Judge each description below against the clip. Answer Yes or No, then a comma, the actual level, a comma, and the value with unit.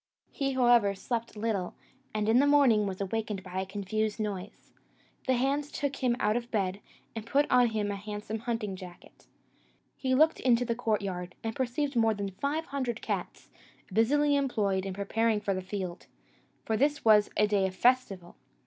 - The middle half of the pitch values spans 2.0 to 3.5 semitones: No, average, 4.0 semitones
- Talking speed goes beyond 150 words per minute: Yes, average, 175 wpm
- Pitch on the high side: Yes, high, 220 Hz